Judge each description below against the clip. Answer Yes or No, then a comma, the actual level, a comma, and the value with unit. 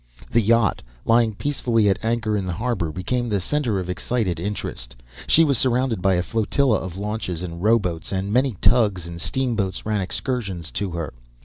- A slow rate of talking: No, average, 180 wpm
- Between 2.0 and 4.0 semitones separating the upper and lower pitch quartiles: No, average, 4.5 semitones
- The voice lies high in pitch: No, low, 105 Hz